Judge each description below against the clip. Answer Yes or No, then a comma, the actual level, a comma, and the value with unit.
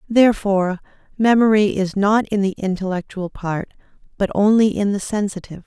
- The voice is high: Yes, high, 200 Hz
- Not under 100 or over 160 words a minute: Yes, average, 140 wpm